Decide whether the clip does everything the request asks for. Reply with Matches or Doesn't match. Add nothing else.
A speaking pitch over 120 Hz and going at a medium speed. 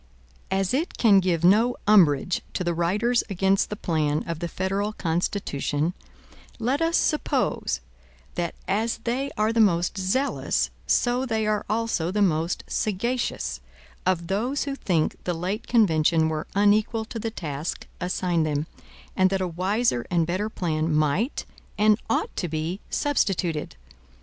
Matches